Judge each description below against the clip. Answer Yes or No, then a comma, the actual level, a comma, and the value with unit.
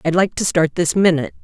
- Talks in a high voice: No, medium, 170 Hz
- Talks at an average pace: No, fast, 250 wpm